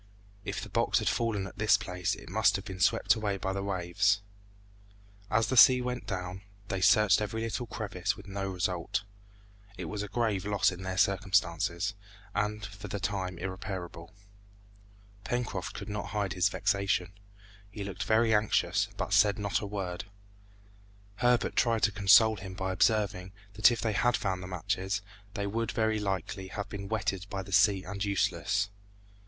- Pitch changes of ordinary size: No, narrow, 2.2 semitones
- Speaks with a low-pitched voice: Yes, low, 100 Hz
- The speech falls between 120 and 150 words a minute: No, average, 170 wpm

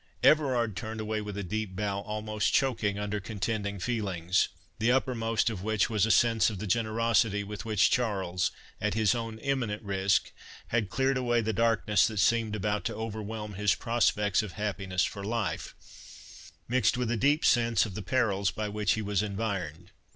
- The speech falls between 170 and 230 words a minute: Yes, average, 175 wpm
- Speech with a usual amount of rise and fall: No, narrow, 2.2 semitones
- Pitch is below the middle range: Yes, low, 105 Hz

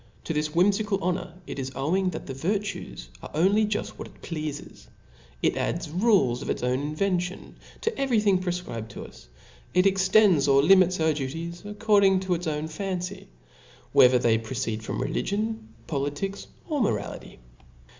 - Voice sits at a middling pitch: Yes, medium, 175 Hz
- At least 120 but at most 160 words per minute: No, average, 170 wpm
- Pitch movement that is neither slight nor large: No, wide, 5.8 semitones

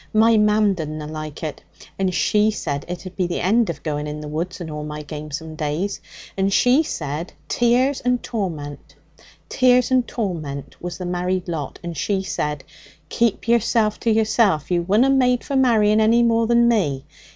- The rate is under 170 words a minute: No, average, 175 wpm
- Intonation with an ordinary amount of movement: No, wide, 6.9 semitones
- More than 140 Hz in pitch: Yes, medium, 185 Hz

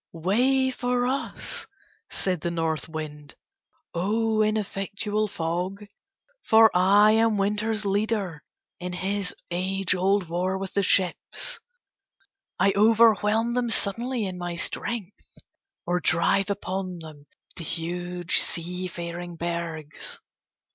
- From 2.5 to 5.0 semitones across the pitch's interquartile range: Yes, average, 3.6 semitones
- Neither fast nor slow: No, slow, 110 wpm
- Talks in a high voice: Yes, high, 195 Hz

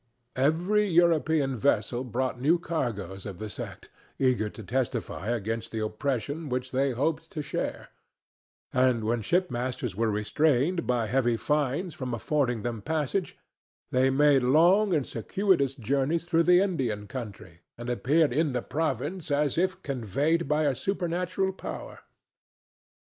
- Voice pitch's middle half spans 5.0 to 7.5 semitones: Yes, average, 5.3 semitones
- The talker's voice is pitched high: No, low, 135 Hz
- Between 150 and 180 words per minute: No, average, 140 wpm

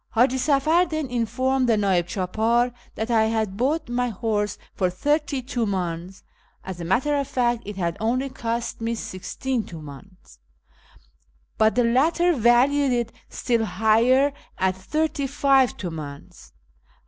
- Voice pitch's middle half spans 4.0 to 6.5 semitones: Yes, average, 5.1 semitones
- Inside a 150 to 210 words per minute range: No, slow, 135 wpm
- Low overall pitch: No, high, 235 Hz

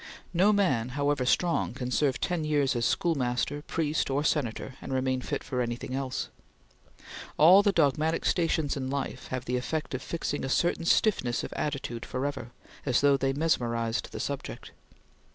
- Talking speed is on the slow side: No, average, 165 wpm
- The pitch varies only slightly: No, average, 3.8 semitones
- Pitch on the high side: No, medium, 140 Hz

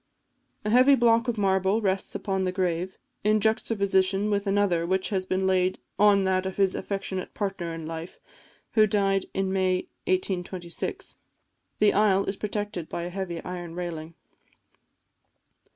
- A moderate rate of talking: Yes, average, 150 wpm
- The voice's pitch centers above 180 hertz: Yes, high, 190 Hz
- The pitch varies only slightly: Yes, narrow, 1.8 semitones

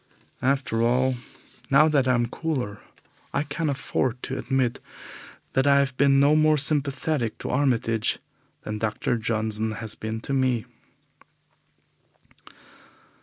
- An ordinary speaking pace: No, slow, 125 wpm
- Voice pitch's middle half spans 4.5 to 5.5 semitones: No, average, 3.5 semitones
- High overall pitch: No, low, 130 Hz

